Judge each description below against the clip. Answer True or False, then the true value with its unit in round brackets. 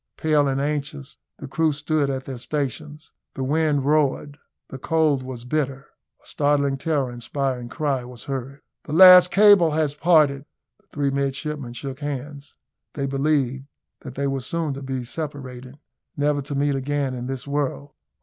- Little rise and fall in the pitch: True (2.1 semitones)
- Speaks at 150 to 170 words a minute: True (160 wpm)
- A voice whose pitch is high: False (140 Hz)